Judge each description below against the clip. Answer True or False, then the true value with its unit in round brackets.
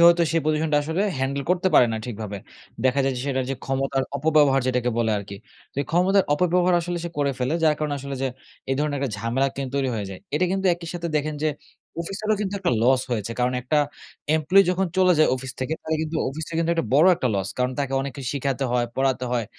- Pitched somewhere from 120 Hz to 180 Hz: True (140 Hz)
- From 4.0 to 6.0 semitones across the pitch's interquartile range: True (4.4 semitones)